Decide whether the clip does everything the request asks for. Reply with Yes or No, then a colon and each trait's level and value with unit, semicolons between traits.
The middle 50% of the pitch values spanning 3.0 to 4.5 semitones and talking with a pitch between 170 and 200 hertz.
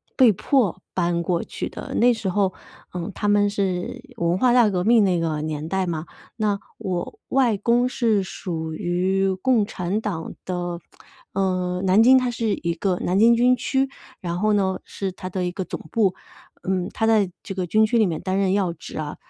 Yes: average, 3.6 semitones; high, 190 Hz